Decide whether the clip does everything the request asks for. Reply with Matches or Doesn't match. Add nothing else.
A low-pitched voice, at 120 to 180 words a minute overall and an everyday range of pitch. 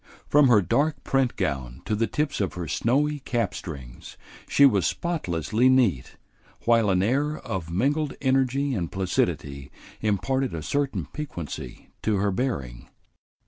Doesn't match